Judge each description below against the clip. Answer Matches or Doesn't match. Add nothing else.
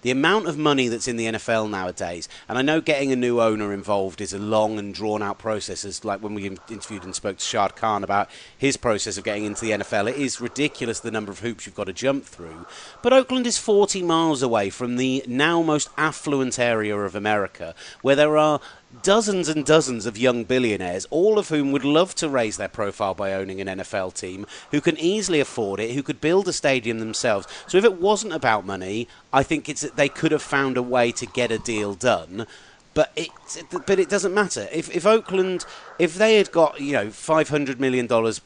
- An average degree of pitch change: Doesn't match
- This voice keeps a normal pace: Doesn't match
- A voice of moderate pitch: Doesn't match